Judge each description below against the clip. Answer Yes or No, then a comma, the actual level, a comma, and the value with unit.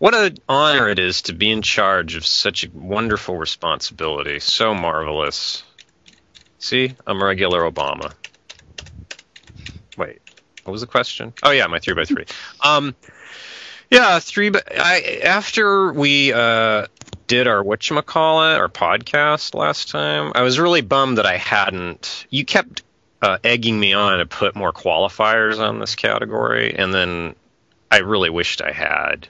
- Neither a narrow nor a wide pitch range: No, wide, 7.8 semitones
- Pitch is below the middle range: Yes, low, 120 Hz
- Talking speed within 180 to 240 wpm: No, average, 150 wpm